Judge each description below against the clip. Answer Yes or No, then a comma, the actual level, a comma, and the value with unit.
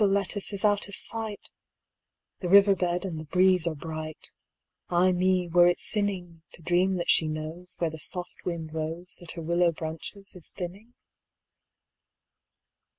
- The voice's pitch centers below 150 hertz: No, medium, 175 Hz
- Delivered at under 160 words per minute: Yes, average, 140 wpm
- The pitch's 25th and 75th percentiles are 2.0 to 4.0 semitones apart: Yes, average, 2.7 semitones